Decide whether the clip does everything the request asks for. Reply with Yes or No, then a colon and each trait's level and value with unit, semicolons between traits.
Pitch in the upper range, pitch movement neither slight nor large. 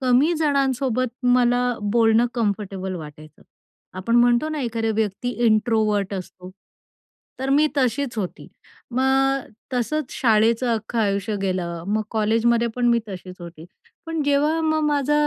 Yes: high, 235 Hz; average, 4.3 semitones